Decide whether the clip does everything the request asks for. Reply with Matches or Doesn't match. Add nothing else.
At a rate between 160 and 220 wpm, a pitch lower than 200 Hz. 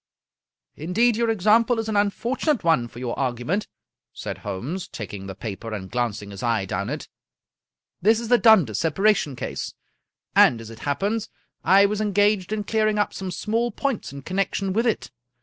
Matches